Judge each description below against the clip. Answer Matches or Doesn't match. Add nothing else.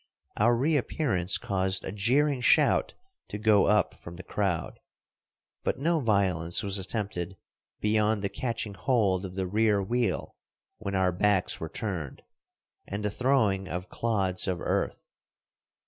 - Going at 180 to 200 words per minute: Doesn't match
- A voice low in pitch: Matches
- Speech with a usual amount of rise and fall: Matches